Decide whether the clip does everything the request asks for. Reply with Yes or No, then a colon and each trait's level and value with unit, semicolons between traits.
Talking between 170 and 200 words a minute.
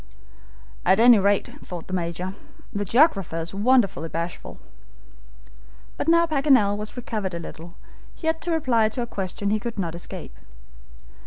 No: average, 155 wpm